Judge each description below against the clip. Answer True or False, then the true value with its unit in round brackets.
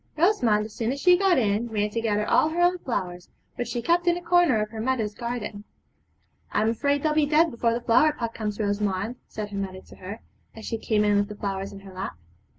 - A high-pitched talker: True (225 Hz)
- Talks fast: True (245 wpm)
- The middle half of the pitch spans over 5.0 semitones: True (5.5 semitones)